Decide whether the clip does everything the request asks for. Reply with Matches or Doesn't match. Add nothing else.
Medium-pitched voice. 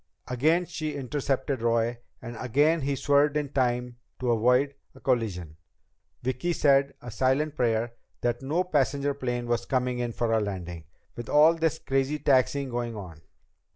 Doesn't match